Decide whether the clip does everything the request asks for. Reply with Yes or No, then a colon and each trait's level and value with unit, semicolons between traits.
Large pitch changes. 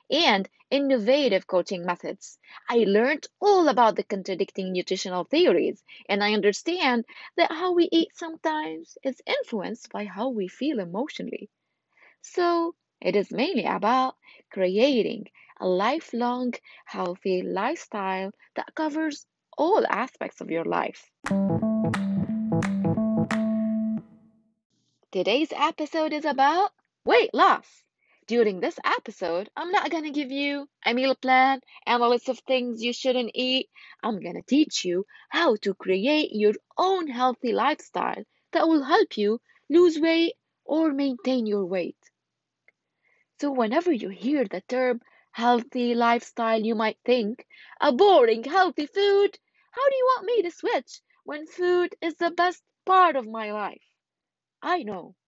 Yes: wide, 7.1 semitones